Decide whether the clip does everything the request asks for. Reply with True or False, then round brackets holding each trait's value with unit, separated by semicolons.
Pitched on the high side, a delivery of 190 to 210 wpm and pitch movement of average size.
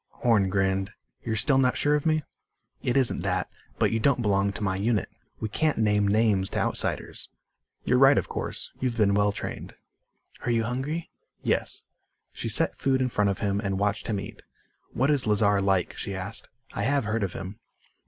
False (105 Hz; 195 wpm; 4.1 semitones)